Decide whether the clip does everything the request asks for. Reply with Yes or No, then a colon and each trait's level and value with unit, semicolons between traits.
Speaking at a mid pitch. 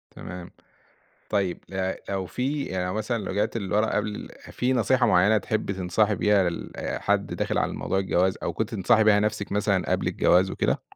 No: low, 105 Hz